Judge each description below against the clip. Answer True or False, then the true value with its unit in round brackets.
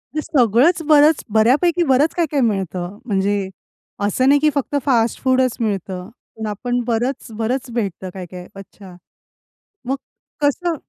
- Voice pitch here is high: True (240 Hz)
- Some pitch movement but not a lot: False (6.1 semitones)